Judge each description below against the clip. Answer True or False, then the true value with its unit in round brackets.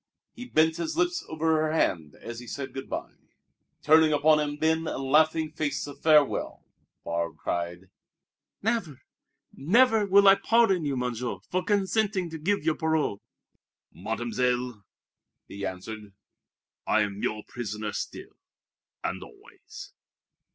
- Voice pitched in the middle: True (150 Hz)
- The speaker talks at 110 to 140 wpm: True (135 wpm)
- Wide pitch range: True (6.1 semitones)